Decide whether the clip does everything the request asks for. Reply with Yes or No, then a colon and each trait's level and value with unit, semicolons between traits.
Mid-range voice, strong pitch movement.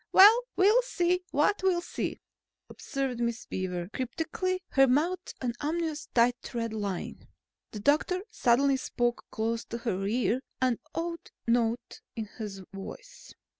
No: very high, 255 Hz; wide, 7.0 semitones